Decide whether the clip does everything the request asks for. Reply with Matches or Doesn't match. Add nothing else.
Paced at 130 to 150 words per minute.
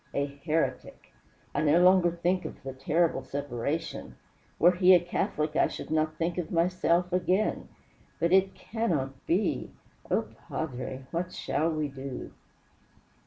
Matches